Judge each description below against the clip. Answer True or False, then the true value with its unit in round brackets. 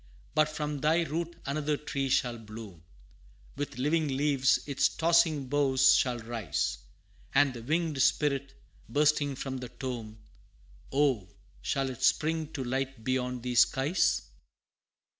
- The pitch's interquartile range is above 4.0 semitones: False (3.0 semitones)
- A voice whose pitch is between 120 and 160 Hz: True (135 Hz)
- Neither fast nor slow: False (130 wpm)